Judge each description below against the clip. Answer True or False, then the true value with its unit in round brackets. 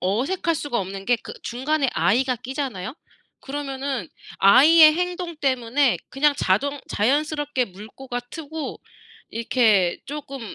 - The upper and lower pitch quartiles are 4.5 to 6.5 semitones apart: False (4.0 semitones)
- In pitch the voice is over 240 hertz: True (265 Hz)